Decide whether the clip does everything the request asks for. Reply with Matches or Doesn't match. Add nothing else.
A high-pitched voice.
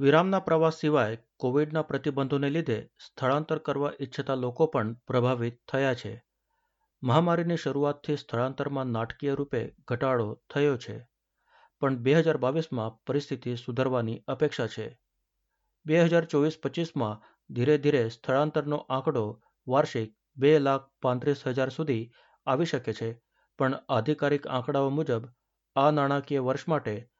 Doesn't match